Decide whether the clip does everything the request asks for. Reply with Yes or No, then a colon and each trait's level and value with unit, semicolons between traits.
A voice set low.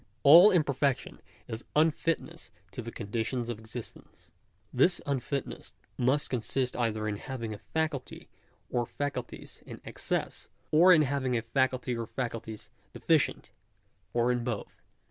Yes: low, 125 Hz